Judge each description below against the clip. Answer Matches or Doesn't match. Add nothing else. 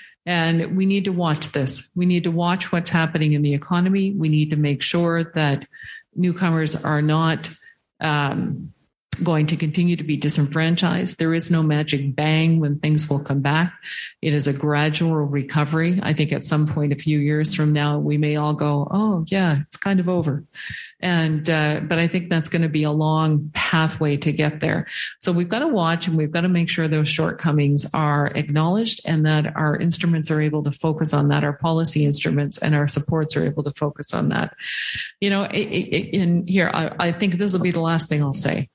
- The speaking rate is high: Matches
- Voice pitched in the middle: Matches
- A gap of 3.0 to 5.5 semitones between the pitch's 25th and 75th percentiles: Doesn't match